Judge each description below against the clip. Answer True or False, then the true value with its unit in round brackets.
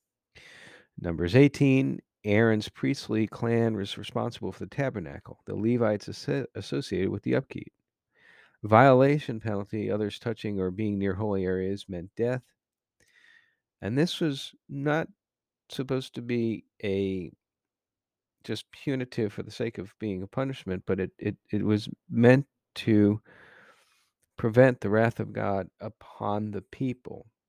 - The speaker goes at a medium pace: False (130 wpm)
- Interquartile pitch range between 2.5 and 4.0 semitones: False (4.4 semitones)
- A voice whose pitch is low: True (110 Hz)